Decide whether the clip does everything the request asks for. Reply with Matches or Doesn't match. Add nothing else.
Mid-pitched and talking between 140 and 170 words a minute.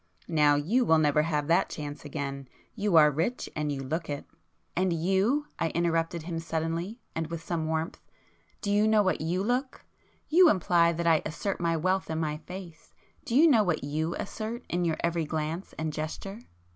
Doesn't match